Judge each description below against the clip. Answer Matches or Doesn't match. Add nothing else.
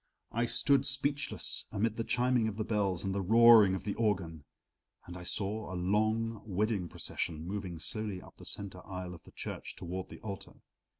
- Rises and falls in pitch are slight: Doesn't match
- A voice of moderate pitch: Doesn't match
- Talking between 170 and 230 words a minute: Matches